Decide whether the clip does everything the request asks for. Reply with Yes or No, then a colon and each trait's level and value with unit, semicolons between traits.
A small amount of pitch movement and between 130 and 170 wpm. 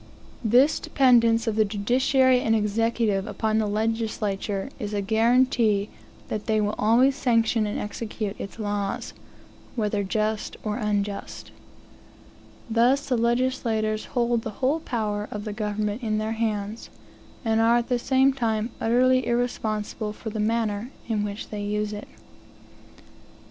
Yes: narrow, 2.3 semitones; average, 140 wpm